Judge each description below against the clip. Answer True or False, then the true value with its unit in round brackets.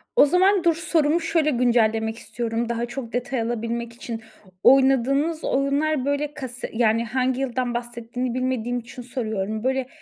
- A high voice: True (250 Hz)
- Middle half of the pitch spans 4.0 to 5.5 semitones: False (3.0 semitones)